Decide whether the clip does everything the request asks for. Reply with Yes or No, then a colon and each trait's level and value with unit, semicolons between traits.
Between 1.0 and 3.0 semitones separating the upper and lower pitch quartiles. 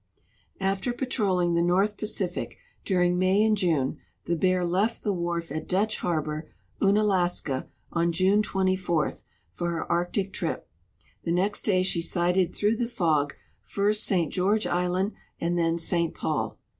Yes: average, 2.7 semitones